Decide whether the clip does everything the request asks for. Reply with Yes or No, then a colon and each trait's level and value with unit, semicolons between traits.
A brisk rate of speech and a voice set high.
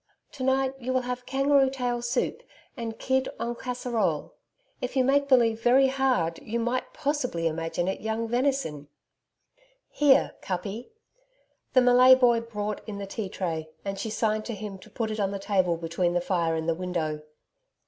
No: average, 175 wpm; high, 230 Hz